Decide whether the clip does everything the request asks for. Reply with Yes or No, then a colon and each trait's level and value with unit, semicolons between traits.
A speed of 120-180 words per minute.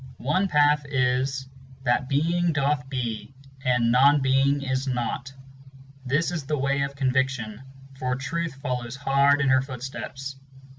Yes: average, 140 wpm